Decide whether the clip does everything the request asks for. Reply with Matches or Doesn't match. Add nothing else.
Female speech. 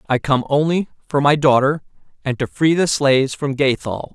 Doesn't match